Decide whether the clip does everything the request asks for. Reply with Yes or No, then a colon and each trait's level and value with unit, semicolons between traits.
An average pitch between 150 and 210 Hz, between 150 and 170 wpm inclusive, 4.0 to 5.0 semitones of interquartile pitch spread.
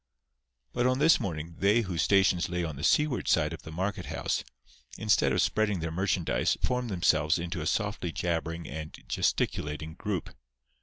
No: very low, 90 Hz; average, 165 wpm; average, 4.3 semitones